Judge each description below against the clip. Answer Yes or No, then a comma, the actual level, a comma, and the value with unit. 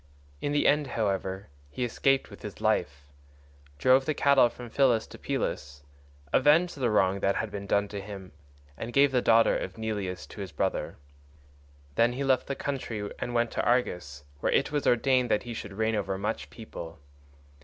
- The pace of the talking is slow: No, average, 180 wpm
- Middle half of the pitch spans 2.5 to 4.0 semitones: No, average, 4.7 semitones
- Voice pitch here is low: Yes, low, 115 Hz